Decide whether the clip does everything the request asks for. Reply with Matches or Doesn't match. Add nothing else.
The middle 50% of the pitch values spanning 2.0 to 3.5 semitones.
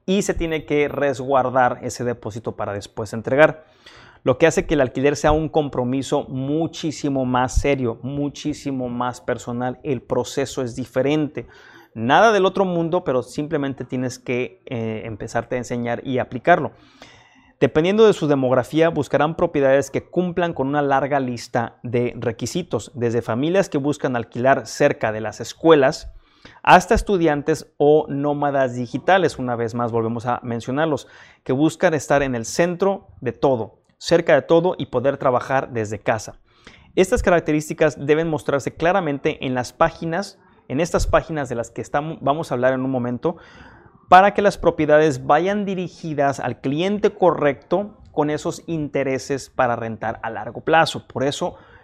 Doesn't match